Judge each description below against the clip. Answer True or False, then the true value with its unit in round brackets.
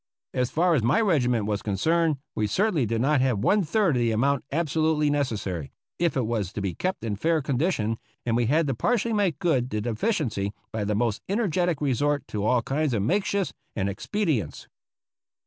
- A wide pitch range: True (7.0 semitones)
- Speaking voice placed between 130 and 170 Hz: True (135 Hz)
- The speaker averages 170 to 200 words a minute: True (190 wpm)